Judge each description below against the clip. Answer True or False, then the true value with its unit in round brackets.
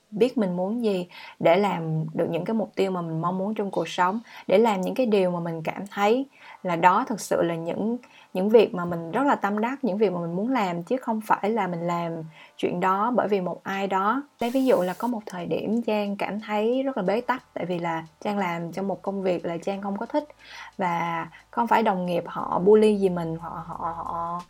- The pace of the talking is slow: False (245 wpm)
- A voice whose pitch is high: True (195 Hz)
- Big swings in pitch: False (4.3 semitones)